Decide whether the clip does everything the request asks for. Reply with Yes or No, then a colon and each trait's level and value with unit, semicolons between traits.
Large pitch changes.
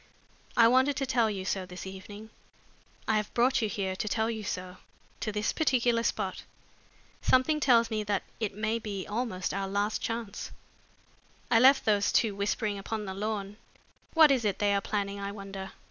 No: average, 2.7 semitones